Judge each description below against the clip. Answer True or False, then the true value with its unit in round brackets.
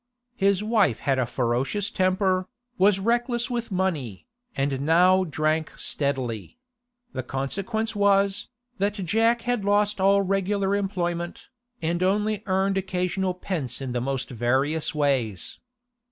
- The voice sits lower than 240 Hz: True (185 Hz)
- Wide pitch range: True (6.3 semitones)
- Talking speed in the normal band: False (125 wpm)